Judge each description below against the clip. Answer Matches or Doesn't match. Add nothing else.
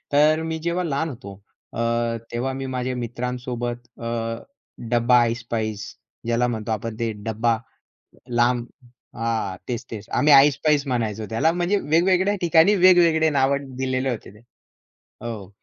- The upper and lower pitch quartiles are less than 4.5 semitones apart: Doesn't match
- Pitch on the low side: Matches